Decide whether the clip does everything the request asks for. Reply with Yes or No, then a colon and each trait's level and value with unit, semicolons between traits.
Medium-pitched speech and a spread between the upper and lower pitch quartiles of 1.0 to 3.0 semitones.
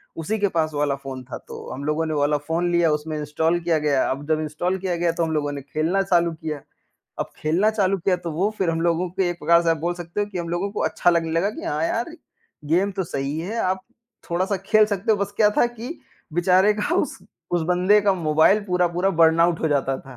No: medium, 170 Hz; average, 3.6 semitones